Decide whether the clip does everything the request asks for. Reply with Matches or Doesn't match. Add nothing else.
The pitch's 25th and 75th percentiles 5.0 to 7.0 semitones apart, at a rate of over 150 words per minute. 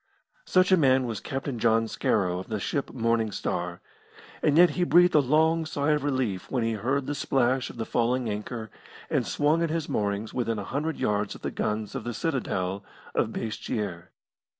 Matches